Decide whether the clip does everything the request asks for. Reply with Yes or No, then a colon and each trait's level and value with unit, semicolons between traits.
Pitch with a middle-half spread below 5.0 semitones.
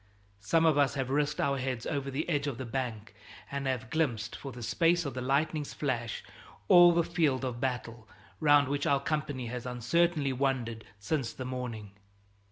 Yes: average, 3.2 semitones